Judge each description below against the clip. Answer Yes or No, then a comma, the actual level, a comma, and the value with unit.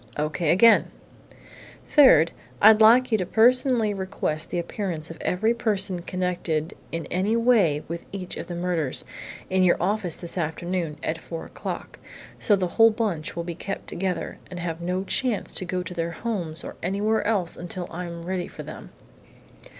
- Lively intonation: No, average, 3.7 semitones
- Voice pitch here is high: No, medium, 180 Hz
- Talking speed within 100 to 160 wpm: No, average, 175 wpm